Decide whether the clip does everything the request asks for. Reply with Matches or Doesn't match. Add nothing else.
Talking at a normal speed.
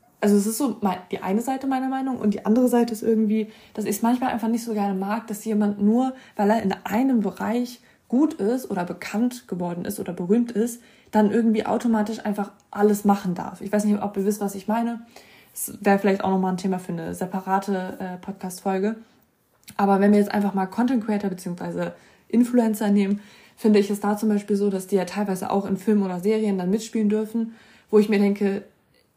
Doesn't match